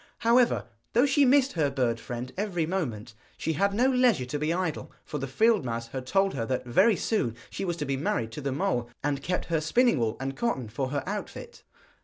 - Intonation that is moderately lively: No, wide, 8.3 semitones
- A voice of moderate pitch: Yes, medium, 150 Hz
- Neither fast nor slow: No, fast, 220 wpm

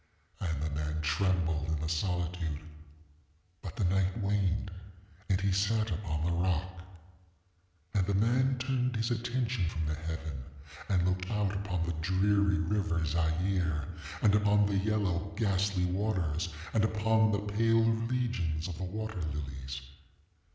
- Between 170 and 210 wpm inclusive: No, average, 140 wpm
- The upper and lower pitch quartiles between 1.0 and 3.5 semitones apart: No, average, 4.5 semitones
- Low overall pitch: Yes, very low, 95 Hz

